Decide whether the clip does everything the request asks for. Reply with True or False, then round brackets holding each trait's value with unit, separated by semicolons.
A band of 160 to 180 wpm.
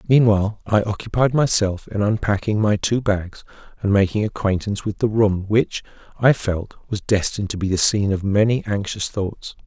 True (175 wpm)